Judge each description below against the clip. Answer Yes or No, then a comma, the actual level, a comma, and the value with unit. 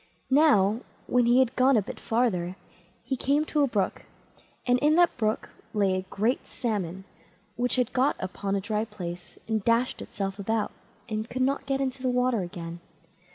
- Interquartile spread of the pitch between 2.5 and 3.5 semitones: No, average, 4.6 semitones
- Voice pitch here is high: Yes, high, 230 Hz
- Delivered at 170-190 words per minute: Yes, average, 180 wpm